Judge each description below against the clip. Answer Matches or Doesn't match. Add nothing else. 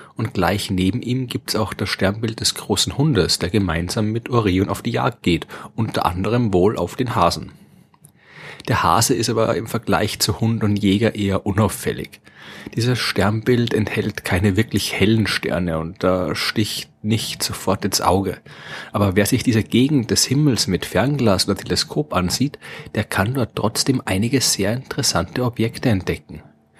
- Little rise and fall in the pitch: Doesn't match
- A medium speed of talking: Matches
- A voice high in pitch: Doesn't match